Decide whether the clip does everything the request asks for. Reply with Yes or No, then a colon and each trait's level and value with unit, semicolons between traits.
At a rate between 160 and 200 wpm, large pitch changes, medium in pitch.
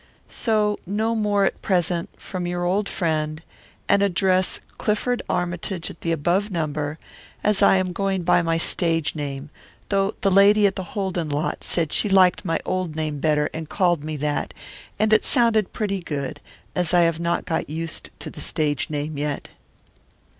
No: average, 170 wpm; average, 4.0 semitones; medium, 175 Hz